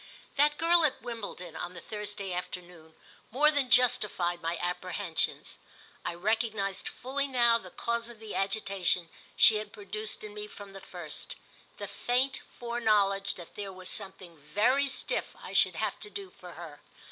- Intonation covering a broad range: No, average, 4.9 semitones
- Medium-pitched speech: No, high, 205 Hz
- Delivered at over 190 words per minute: No, average, 160 wpm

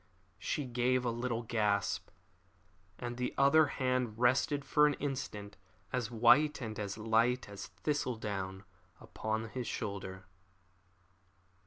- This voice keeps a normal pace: No, slow, 125 wpm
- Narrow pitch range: No, average, 3.1 semitones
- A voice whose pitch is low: Yes, low, 120 Hz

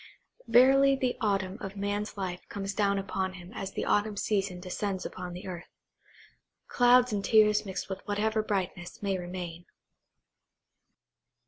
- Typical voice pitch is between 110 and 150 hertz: No, high, 200 Hz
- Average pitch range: No, narrow, 2.3 semitones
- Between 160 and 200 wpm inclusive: No, average, 140 wpm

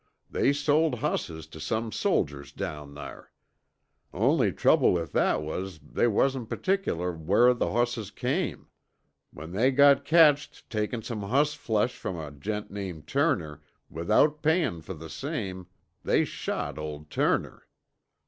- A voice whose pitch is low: Yes, low, 105 Hz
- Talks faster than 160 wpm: No, average, 140 wpm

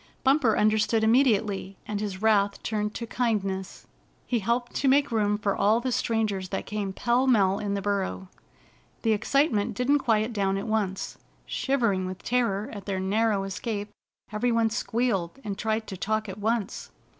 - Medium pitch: No, high, 215 Hz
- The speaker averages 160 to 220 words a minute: Yes, average, 165 wpm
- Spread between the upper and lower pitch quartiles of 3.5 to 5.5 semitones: No, average, 2.8 semitones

